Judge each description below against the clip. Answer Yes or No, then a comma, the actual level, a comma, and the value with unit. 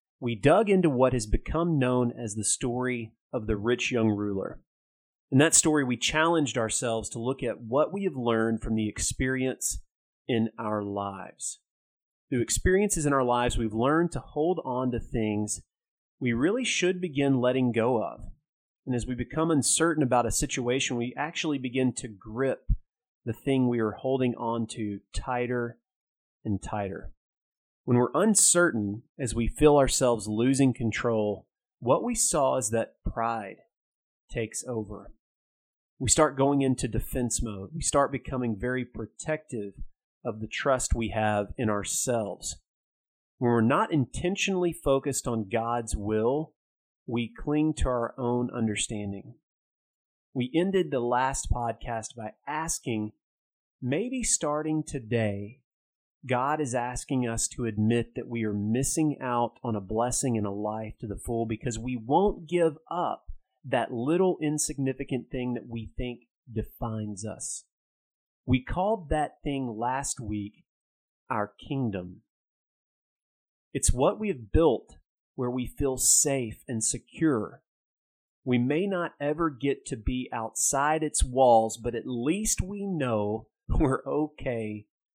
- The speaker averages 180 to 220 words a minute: No, average, 145 wpm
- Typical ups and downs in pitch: Yes, average, 4.3 semitones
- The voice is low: Yes, low, 125 Hz